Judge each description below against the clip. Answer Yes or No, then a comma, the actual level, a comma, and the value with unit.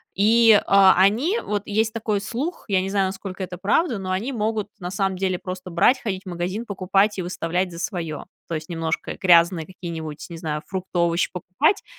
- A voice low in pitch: No, high, 190 Hz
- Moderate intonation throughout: Yes, average, 3.0 semitones